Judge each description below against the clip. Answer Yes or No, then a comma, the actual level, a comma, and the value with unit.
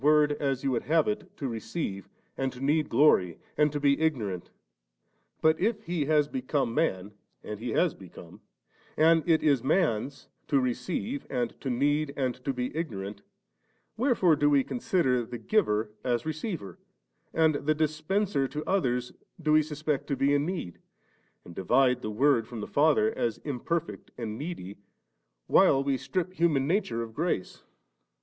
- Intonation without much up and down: No, average, 4.7 semitones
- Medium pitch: Yes, medium, 145 Hz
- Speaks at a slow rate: No, average, 165 wpm